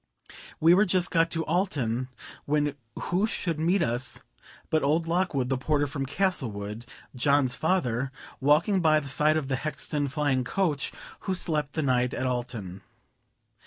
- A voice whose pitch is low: No, medium, 145 Hz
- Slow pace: No, average, 155 wpm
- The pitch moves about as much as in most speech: Yes, average, 4.4 semitones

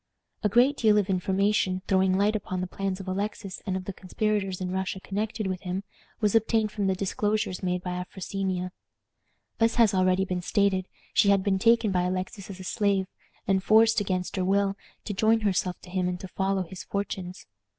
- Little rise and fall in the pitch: Yes, narrow, 2.0 semitones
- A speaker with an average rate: Yes, average, 195 wpm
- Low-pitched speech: No, high, 195 Hz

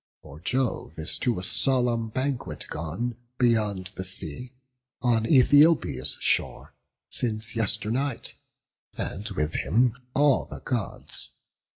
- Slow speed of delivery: Yes, slow, 110 wpm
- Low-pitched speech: Yes, low, 115 Hz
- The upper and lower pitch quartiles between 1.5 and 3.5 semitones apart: No, average, 4.8 semitones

